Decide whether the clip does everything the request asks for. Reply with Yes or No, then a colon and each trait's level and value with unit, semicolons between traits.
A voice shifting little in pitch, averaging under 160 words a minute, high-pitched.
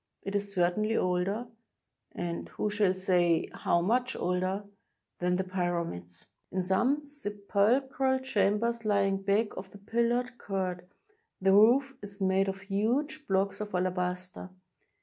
No: average, 3.7 semitones; average, 145 wpm; high, 200 Hz